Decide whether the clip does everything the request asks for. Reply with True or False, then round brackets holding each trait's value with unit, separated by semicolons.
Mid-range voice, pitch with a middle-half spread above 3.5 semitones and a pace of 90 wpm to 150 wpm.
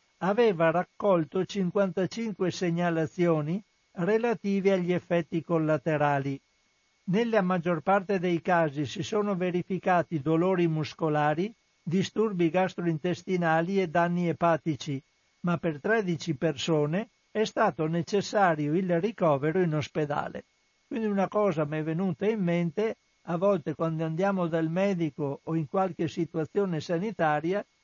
False (175 Hz; 3.2 semitones; 115 wpm)